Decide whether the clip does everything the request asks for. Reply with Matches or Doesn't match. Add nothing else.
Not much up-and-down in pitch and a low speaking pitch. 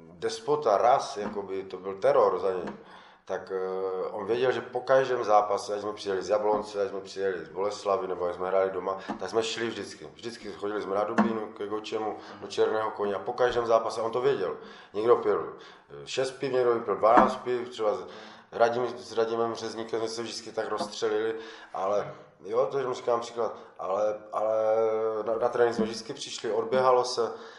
Doesn't match